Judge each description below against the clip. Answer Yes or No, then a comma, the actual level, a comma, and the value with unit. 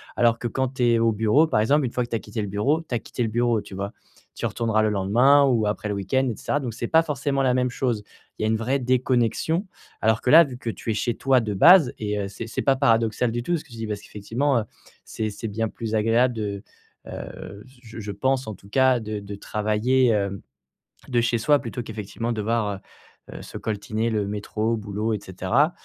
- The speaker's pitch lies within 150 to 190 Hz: No, low, 115 Hz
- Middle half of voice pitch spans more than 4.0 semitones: No, average, 3.3 semitones